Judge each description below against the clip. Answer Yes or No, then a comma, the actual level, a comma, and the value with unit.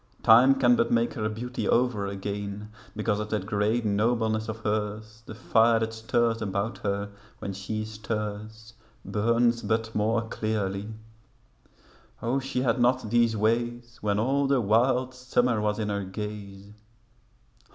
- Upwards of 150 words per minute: No, average, 145 wpm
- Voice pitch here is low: Yes, low, 110 Hz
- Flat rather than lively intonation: Yes, narrow, 2.1 semitones